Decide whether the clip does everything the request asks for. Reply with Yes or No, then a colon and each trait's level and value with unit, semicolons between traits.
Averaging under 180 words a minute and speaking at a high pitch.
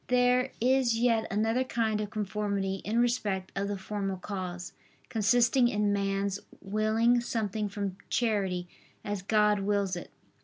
Yes: average, 140 wpm; high, 210 Hz